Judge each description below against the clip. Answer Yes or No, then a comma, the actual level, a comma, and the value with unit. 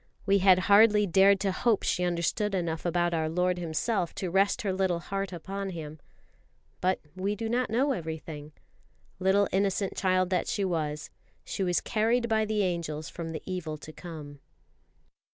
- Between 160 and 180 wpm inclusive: Yes, average, 170 wpm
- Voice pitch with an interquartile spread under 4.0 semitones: Yes, average, 3.0 semitones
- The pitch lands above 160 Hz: Yes, medium, 185 Hz